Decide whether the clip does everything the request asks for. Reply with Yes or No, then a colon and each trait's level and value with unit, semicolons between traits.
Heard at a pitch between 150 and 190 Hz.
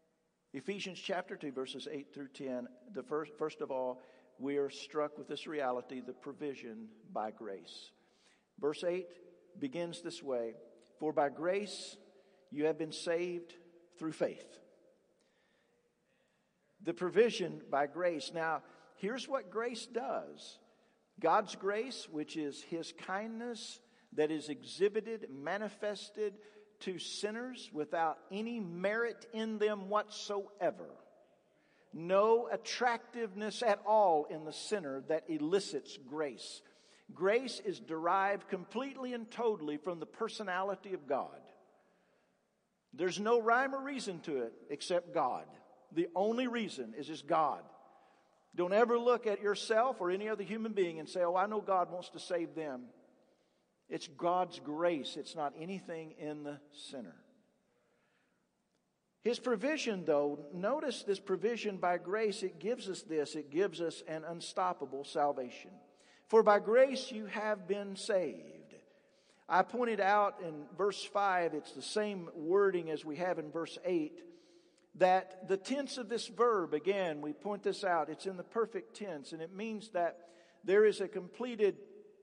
Yes: medium, 185 Hz